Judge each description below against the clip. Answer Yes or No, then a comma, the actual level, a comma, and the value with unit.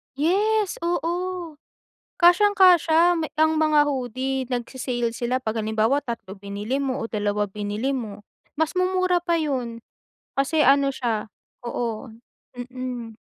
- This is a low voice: No, very high, 265 Hz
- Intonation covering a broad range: Yes, wide, 6.1 semitones